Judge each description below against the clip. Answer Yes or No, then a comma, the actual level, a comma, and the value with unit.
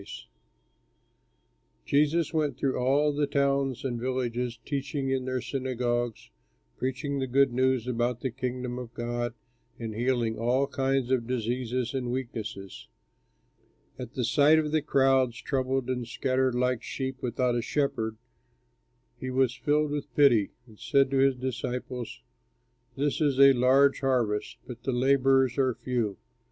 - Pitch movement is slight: Yes, narrow, 2.1 semitones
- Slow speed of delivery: No, average, 145 wpm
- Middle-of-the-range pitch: No, low, 130 Hz